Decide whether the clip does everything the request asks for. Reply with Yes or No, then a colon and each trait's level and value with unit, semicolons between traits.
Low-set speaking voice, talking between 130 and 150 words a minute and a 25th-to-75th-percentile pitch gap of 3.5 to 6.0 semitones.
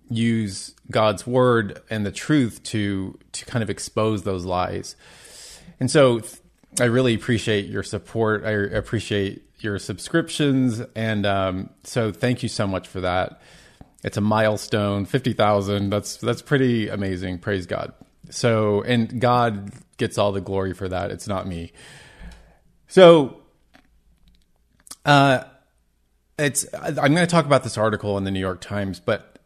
Yes: low, 105 Hz; average, 145 wpm; average, 3.8 semitones